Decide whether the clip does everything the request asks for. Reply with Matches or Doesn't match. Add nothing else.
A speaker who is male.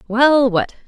Doesn't match